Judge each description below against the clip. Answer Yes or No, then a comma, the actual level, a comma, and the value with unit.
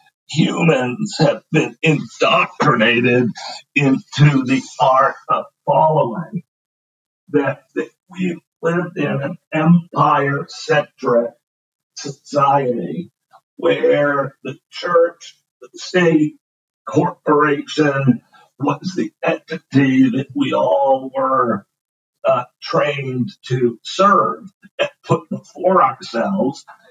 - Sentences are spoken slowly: Yes, slow, 85 wpm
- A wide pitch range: No, average, 4.7 semitones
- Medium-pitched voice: Yes, medium, 150 Hz